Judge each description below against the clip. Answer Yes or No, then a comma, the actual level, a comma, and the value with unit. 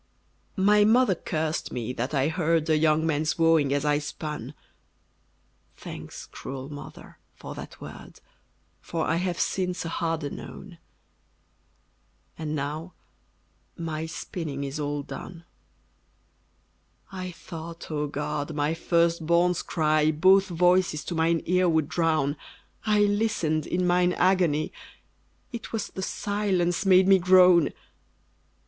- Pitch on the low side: No, medium, 165 Hz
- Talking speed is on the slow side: Yes, slow, 130 wpm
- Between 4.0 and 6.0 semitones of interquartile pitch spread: No, average, 3.1 semitones